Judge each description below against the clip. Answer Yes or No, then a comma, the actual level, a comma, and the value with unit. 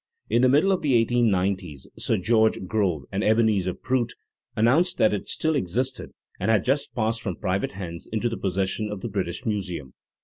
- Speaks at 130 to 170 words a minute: No, average, 190 wpm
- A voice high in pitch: No, low, 110 Hz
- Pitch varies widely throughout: No, average, 4.2 semitones